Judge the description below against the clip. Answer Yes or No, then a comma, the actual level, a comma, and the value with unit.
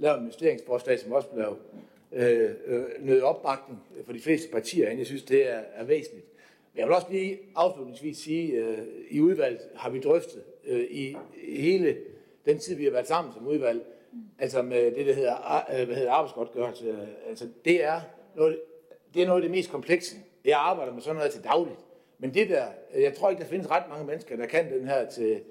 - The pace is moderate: Yes, average, 210 wpm